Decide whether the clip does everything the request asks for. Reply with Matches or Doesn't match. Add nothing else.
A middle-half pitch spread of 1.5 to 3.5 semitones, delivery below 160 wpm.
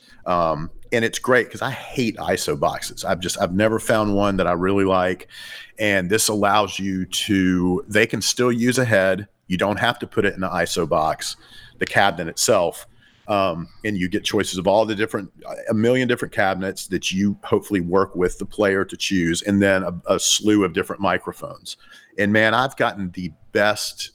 Doesn't match